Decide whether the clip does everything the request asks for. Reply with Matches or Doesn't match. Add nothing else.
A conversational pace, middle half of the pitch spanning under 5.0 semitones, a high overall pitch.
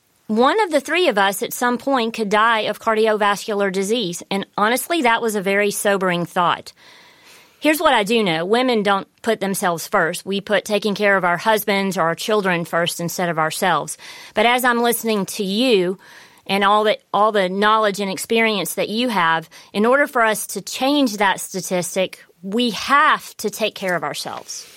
Matches